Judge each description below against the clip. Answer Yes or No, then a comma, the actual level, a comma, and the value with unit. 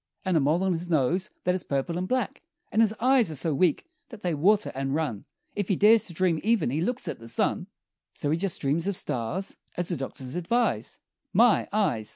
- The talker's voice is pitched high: No, medium, 175 Hz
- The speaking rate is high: Yes, fast, 220 wpm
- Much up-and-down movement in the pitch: Yes, wide, 5.7 semitones